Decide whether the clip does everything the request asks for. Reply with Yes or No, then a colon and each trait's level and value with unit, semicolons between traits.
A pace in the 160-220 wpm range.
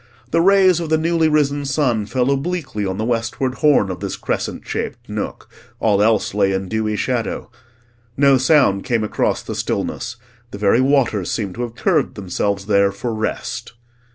Yes: average, 175 wpm